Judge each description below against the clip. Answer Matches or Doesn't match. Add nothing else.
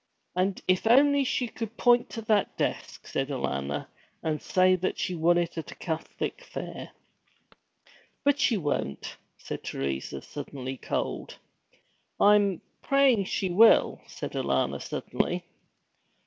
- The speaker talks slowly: Matches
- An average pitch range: Doesn't match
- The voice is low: Doesn't match